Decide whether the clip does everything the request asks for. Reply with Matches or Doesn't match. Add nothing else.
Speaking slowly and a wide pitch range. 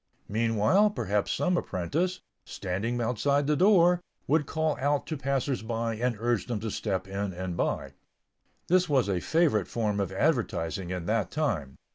Doesn't match